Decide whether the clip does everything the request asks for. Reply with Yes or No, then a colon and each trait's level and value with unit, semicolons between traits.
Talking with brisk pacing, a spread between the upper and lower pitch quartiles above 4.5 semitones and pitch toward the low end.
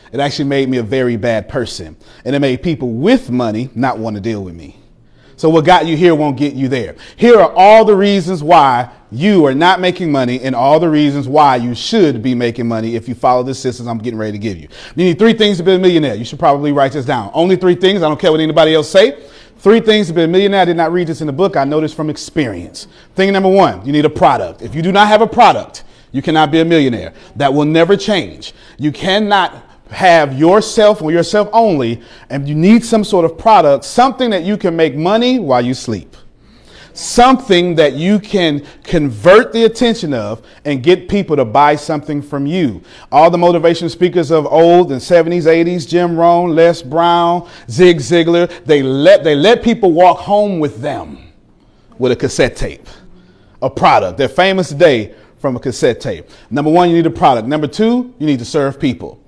No: fast, 220 wpm; average, 5.1 semitones; medium, 160 Hz